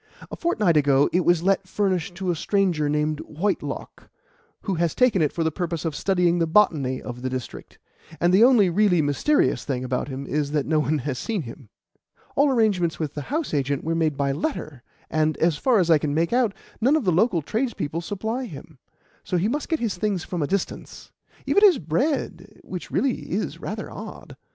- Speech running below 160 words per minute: No, fast, 205 wpm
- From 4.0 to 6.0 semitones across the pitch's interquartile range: Yes, wide, 5.6 semitones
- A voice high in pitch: No, medium, 170 Hz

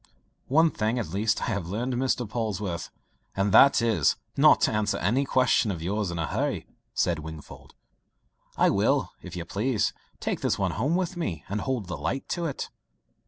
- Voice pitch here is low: Yes, low, 110 Hz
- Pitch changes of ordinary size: No, wide, 5.7 semitones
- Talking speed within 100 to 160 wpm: No, average, 185 wpm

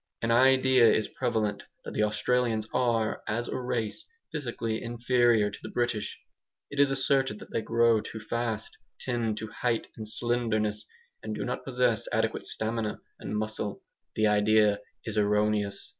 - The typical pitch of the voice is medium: No, low, 115 Hz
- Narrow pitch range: Yes, narrow, 2.2 semitones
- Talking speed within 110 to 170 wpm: Yes, average, 155 wpm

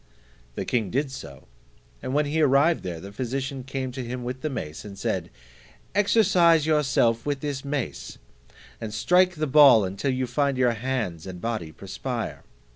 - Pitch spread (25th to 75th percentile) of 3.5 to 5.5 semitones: Yes, average, 4.4 semitones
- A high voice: No, low, 130 Hz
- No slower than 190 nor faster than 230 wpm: No, average, 170 wpm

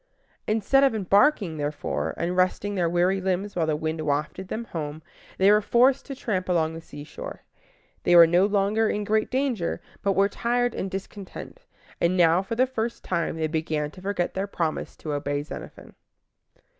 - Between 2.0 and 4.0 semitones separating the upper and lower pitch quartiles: No, average, 4.6 semitones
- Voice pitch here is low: No, medium, 185 Hz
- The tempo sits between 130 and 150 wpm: No, average, 180 wpm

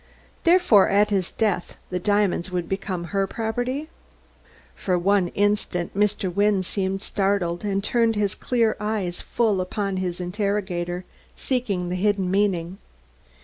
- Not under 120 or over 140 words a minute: Yes, slow, 135 wpm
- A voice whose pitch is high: Yes, high, 195 Hz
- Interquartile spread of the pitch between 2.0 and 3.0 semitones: Yes, narrow, 2.5 semitones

